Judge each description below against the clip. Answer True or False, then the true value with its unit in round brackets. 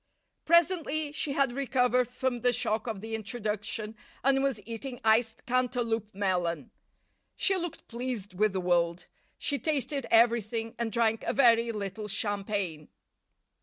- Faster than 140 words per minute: False (135 wpm)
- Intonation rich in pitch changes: False (3.4 semitones)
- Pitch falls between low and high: False (230 Hz)